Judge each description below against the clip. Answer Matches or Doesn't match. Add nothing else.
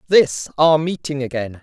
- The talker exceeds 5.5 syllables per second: Doesn't match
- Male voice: Matches